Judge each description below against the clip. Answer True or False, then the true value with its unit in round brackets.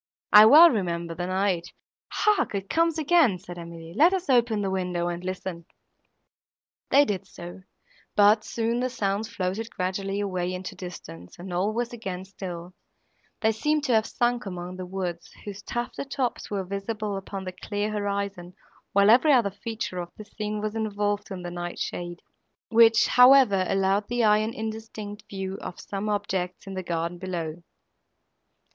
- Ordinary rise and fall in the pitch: True (3.4 semitones)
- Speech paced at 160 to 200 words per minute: True (165 wpm)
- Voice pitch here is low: False (200 Hz)